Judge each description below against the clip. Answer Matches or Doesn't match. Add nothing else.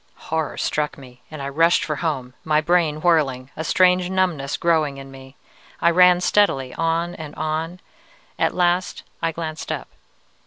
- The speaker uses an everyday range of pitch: Matches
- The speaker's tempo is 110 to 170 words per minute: Matches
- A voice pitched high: Doesn't match